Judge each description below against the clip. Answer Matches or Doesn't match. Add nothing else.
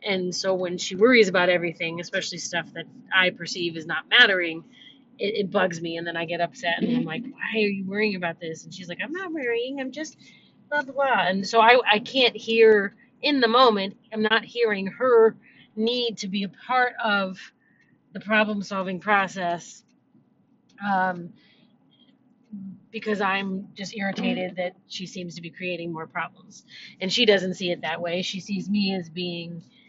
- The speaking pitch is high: Matches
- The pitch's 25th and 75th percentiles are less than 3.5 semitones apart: Doesn't match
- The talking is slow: Doesn't match